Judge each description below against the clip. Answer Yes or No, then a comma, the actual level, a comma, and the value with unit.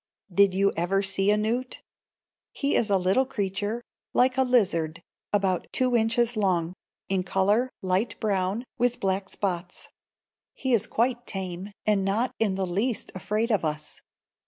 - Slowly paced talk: No, average, 155 wpm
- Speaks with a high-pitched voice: Yes, high, 200 Hz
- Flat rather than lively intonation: No, average, 3.8 semitones